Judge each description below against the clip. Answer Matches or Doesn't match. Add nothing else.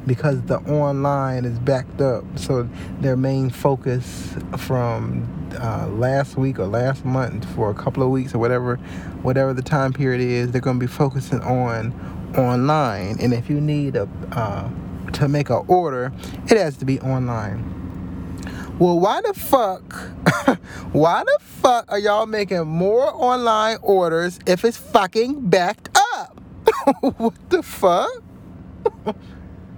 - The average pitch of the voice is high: Doesn't match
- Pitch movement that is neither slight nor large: Doesn't match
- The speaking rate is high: Doesn't match